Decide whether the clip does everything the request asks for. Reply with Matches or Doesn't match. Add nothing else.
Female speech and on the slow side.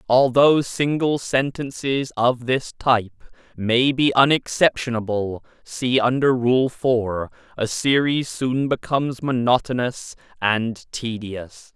Doesn't match